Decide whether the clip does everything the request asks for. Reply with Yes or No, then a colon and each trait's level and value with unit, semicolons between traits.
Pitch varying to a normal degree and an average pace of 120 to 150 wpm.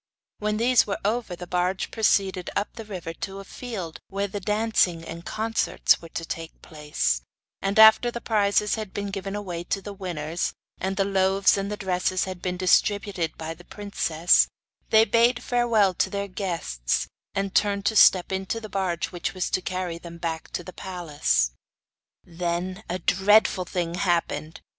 No: average, 3.0 semitones; average, 175 wpm